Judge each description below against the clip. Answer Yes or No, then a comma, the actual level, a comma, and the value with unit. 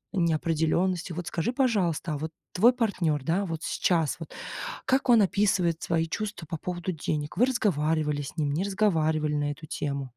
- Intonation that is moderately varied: Yes, average, 3.9 semitones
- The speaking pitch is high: No, medium, 165 Hz